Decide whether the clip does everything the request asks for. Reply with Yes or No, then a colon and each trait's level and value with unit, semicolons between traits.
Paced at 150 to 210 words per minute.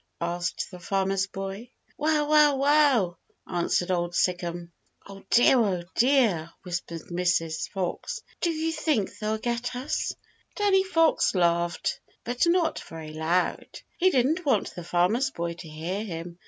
No: average, 140 wpm